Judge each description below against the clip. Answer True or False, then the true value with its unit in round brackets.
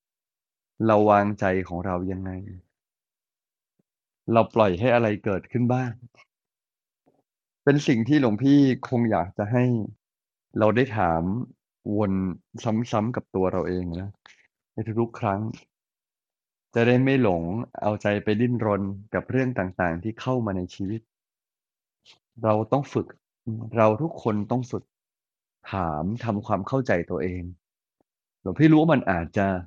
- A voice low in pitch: True (110 Hz)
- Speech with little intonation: False (4.1 semitones)